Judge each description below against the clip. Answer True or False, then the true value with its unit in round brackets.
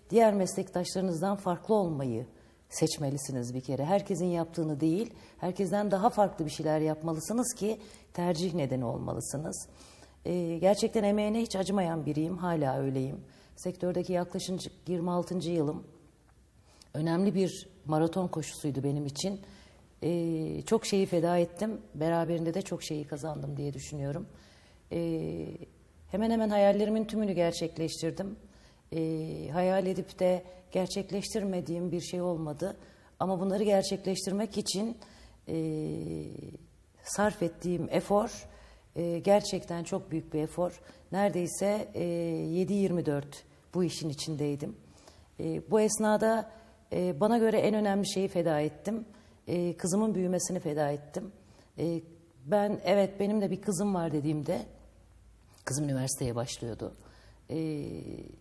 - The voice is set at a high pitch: False (175 Hz)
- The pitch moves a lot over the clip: False (4.2 semitones)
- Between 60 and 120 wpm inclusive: True (115 wpm)